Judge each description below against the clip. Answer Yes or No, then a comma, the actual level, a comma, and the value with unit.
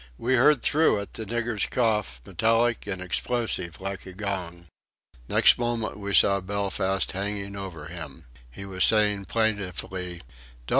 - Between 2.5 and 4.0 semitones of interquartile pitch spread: Yes, average, 3.2 semitones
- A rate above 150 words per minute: No, average, 145 wpm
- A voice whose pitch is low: Yes, low, 100 Hz